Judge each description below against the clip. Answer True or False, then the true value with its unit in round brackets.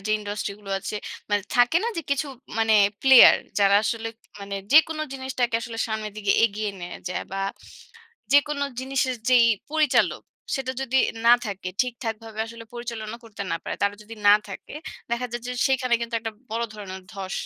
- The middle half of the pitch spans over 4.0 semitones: False (3.7 semitones)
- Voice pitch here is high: True (230 Hz)